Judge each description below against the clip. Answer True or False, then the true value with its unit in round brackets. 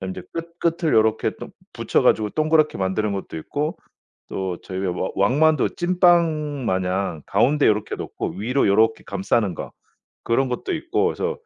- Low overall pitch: True (110 Hz)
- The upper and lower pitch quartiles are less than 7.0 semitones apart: False (8.0 semitones)